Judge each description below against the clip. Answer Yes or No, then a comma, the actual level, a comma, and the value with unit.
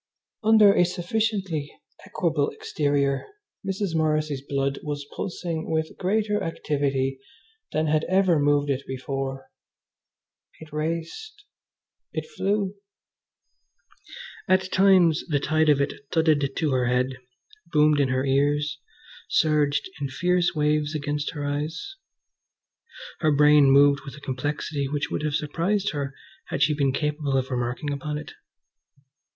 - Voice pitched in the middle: Yes, medium, 150 Hz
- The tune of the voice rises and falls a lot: No, average, 3.1 semitones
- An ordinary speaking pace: No, slow, 130 wpm